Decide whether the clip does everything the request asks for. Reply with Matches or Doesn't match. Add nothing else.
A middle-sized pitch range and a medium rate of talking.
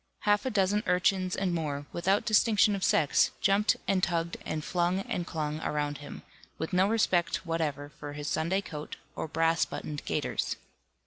Matches